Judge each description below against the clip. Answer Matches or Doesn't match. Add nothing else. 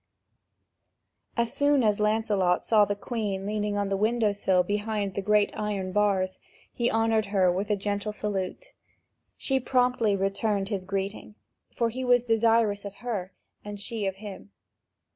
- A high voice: Matches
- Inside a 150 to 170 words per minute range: Matches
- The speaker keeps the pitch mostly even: Matches